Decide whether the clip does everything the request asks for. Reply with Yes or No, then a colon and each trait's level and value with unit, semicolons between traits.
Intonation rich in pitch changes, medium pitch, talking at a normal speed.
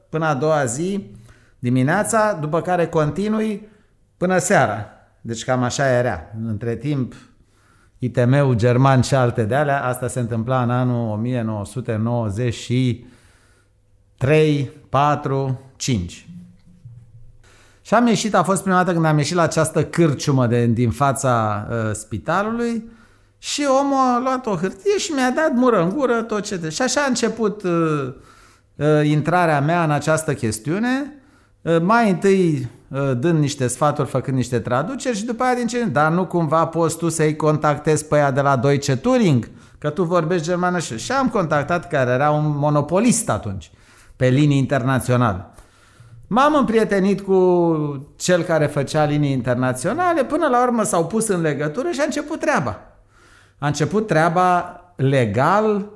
Yes: wide, 7.1 semitones; medium, 150 Hz; average, 150 wpm